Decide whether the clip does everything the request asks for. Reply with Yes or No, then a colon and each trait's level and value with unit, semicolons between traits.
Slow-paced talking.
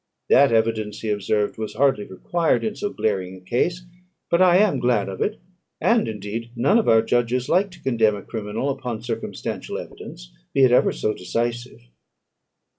No: average, 175 wpm